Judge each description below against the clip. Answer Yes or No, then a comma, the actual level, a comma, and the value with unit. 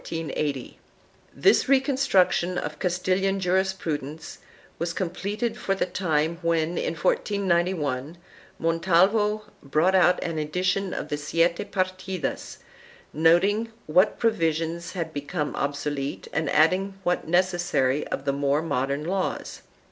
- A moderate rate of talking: No, slow, 120 wpm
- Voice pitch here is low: No, medium, 170 Hz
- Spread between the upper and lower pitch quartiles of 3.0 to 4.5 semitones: Yes, average, 3.7 semitones